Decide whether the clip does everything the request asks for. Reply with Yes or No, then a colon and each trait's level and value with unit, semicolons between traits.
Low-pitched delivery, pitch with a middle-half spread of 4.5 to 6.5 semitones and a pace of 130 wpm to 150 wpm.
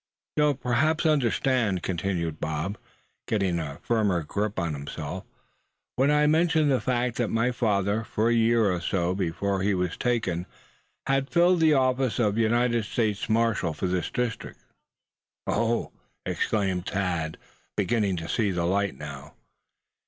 Yes: low, 105 Hz; average, 5.3 semitones; average, 145 wpm